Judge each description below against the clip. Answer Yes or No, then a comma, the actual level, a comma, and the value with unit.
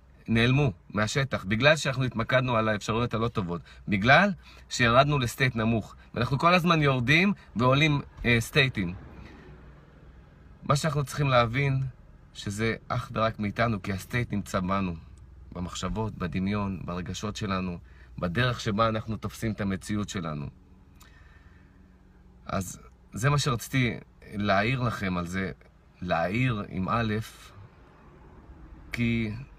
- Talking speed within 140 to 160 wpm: No, average, 110 wpm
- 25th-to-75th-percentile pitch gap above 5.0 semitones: Yes, wide, 5.4 semitones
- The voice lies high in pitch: No, low, 110 Hz